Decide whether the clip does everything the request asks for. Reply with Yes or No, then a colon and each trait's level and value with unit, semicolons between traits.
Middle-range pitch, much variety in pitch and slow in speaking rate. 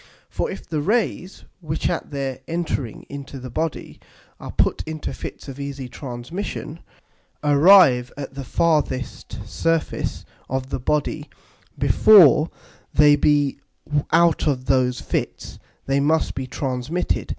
No: medium, 145 Hz; average, 3.4 semitones; slow, 130 wpm